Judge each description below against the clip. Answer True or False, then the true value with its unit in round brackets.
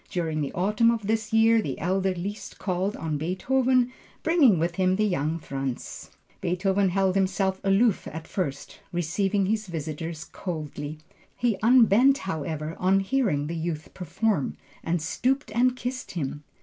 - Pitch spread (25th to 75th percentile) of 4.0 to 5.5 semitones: True (5.1 semitones)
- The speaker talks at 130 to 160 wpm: True (150 wpm)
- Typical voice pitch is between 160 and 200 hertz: True (190 Hz)